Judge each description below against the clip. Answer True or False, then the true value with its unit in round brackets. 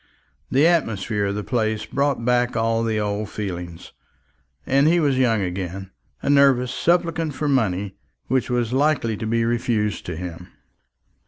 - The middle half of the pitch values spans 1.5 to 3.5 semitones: False (4.7 semitones)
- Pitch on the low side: True (115 Hz)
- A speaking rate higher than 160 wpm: False (155 wpm)